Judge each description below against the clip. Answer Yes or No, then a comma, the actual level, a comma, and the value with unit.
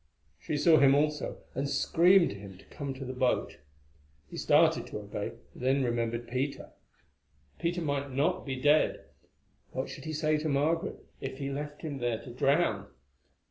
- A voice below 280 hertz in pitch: Yes, medium, 140 Hz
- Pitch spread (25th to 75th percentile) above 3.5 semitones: No, average, 3.1 semitones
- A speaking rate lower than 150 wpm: No, average, 170 wpm